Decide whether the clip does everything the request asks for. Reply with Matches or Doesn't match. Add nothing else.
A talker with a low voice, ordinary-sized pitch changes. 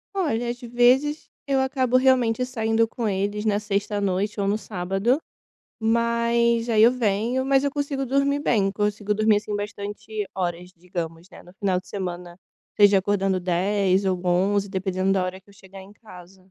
Doesn't match